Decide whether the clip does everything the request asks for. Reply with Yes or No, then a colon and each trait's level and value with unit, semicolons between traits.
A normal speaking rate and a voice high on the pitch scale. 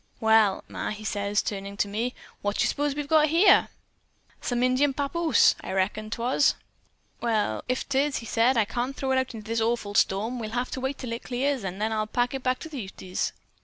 No: fast, 220 wpm; high, 240 Hz